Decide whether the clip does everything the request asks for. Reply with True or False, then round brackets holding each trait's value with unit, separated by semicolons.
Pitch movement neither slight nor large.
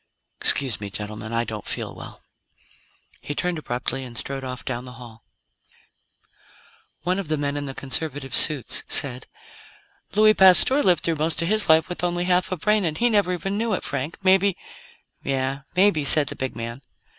False (6.0 semitones)